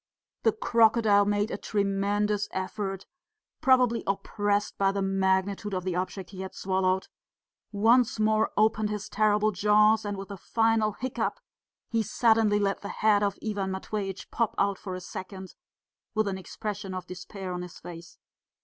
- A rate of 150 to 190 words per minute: Yes, average, 160 wpm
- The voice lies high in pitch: Yes, high, 205 Hz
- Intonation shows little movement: Yes, narrow, 2.1 semitones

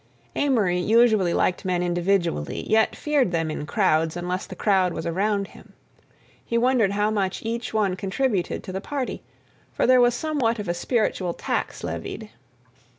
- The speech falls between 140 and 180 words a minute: Yes, average, 160 wpm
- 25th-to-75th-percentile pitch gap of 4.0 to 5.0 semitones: Yes, average, 4.6 semitones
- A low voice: No, high, 200 Hz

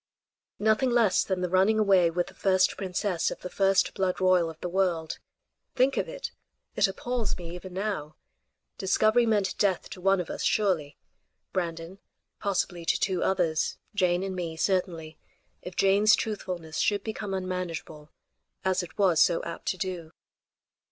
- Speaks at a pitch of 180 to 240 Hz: Yes, medium, 185 Hz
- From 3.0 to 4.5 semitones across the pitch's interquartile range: No, narrow, 2.5 semitones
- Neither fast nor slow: Yes, average, 160 wpm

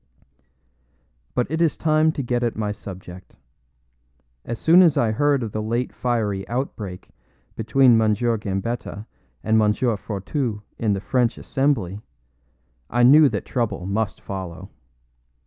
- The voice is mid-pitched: No, low, 115 Hz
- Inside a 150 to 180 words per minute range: No, slow, 135 wpm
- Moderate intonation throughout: Yes, average, 3.8 semitones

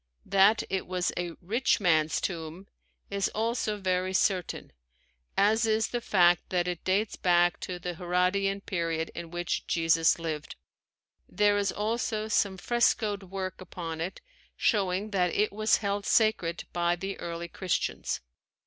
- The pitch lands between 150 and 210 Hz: Yes, medium, 185 Hz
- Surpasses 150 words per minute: No, average, 145 wpm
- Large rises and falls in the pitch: No, average, 2.9 semitones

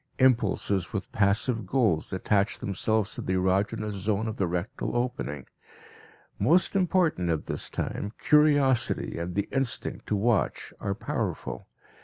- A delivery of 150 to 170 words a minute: No, slow, 135 wpm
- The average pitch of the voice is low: Yes, low, 105 Hz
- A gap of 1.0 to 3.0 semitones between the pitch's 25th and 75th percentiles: No, average, 4.6 semitones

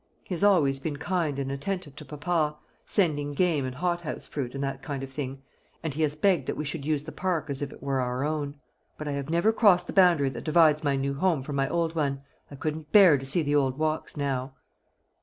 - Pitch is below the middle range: No, medium, 150 Hz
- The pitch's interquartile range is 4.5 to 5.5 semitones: No, average, 3.2 semitones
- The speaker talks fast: Yes, fast, 235 wpm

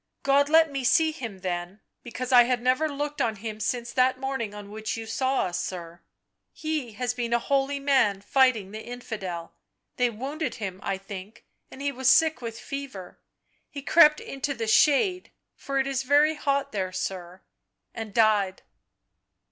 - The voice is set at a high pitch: Yes, high, 245 Hz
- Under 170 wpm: No, average, 175 wpm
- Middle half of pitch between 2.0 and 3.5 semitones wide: No, average, 5.0 semitones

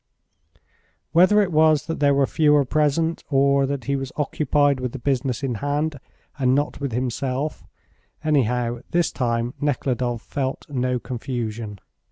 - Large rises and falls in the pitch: No, average, 2.9 semitones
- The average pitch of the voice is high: No, low, 135 Hz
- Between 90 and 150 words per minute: Yes, average, 145 wpm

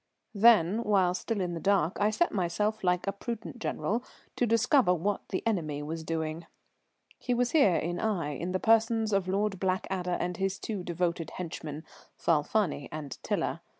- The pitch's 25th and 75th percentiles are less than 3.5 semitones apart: No, average, 4.3 semitones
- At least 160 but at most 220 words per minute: Yes, average, 170 wpm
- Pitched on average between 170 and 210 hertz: Yes, high, 190 Hz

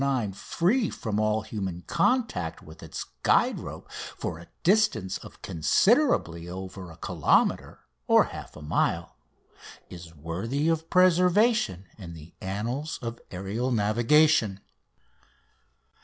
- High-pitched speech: No, low, 110 Hz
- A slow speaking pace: Yes, slow, 110 wpm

